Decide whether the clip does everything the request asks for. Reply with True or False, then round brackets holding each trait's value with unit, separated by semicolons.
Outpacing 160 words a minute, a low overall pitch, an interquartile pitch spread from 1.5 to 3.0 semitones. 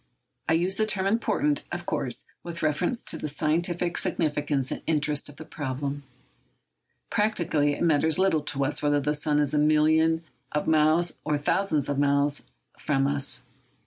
False (175 wpm; 150 Hz; 2.7 semitones)